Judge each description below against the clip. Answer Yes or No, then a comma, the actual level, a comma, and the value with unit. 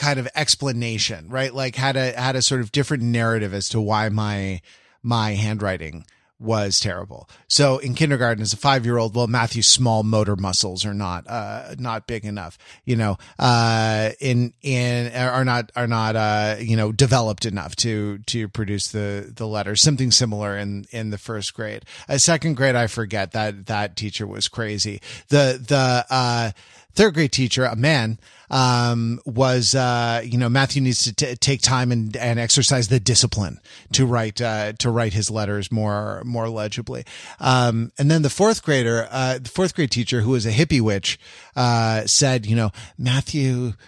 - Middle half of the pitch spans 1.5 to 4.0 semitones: Yes, average, 3.3 semitones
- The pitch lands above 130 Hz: No, low, 120 Hz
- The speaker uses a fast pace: No, average, 175 wpm